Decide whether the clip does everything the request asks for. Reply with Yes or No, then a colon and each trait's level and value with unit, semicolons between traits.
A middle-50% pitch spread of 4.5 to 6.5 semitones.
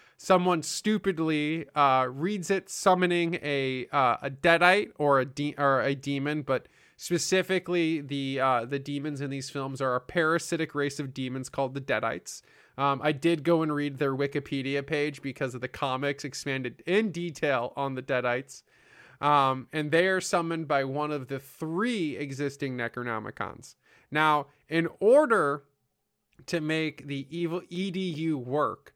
No: average, 3.5 semitones